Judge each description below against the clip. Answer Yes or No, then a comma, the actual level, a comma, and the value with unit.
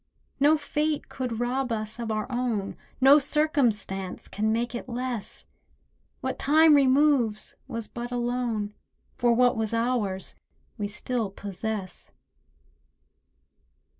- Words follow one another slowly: Yes, slow, 120 wpm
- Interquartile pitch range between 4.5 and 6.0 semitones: No, average, 3.4 semitones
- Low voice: No, high, 240 Hz